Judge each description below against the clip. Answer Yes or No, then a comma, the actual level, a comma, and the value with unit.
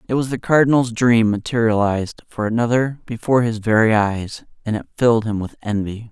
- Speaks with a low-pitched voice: Yes, low, 115 Hz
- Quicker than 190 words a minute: No, average, 175 wpm